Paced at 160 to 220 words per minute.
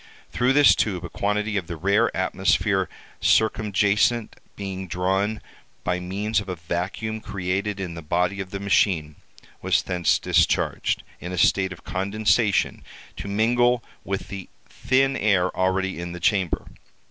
No: average, 145 wpm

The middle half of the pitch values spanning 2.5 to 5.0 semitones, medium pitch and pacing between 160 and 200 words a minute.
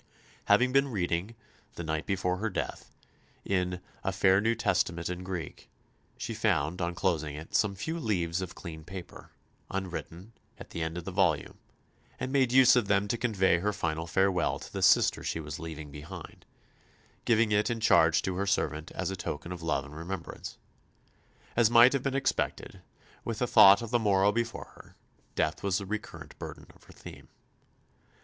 No: average, 4.5 semitones; very low, 95 Hz; average, 180 wpm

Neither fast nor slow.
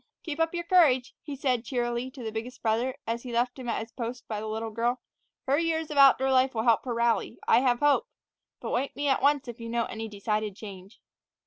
No: fast, 235 wpm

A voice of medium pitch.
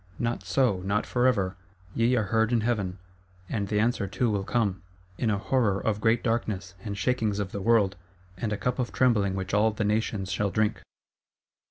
No: low, 105 Hz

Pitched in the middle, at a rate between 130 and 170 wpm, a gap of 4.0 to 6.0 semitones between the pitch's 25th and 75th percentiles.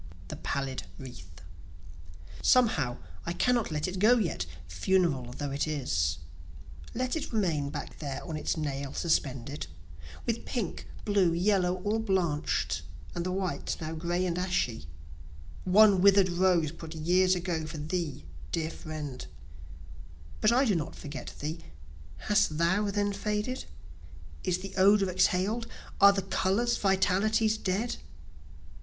Yes: medium, 180 Hz; slow, 135 wpm; average, 4.9 semitones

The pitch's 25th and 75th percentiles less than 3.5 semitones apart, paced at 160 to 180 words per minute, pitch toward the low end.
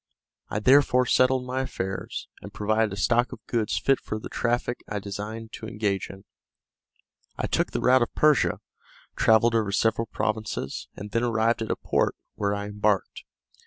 Yes: average, 2.7 semitones; average, 170 wpm; low, 110 Hz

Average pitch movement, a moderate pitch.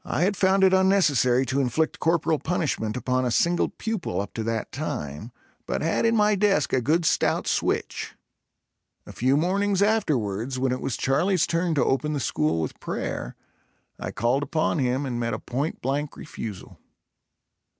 No: wide, 6.1 semitones; medium, 145 Hz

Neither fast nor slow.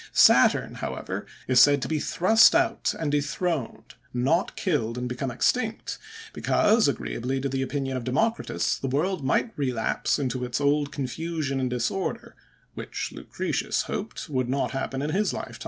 Yes: average, 155 wpm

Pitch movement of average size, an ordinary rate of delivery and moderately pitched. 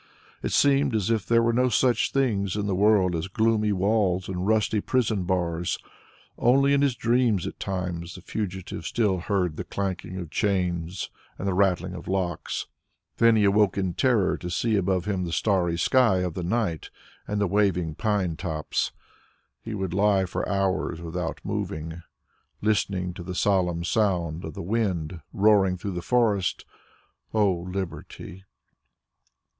No: average, 3.2 semitones; average, 160 wpm; very low, 95 Hz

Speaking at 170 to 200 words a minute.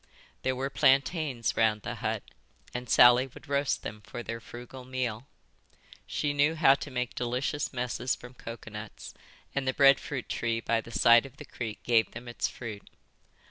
Yes: average, 175 wpm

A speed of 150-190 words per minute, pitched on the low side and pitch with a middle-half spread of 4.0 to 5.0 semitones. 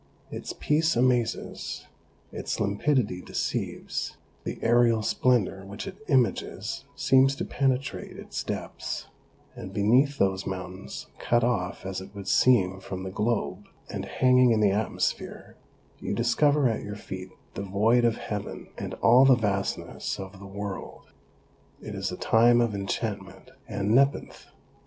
No: average, 140 wpm; low, 110 Hz; average, 4.4 semitones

